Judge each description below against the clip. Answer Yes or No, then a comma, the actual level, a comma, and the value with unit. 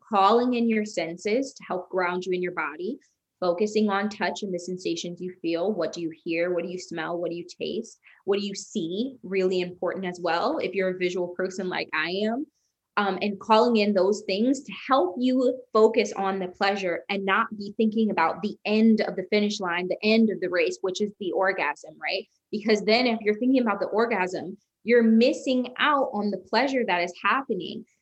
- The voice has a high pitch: Yes, high, 195 Hz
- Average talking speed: No, fast, 210 wpm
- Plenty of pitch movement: No, average, 3.6 semitones